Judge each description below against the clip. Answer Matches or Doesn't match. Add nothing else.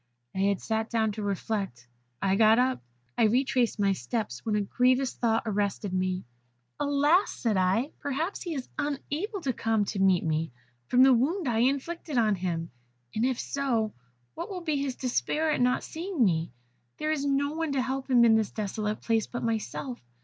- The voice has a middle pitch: Doesn't match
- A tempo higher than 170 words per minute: Matches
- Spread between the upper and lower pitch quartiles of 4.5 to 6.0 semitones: Matches